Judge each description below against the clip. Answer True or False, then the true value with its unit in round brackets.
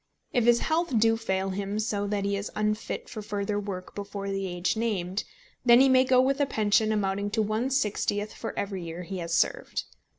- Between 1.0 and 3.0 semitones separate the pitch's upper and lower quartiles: True (2.6 semitones)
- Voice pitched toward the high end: True (205 Hz)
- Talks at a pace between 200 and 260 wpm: True (205 wpm)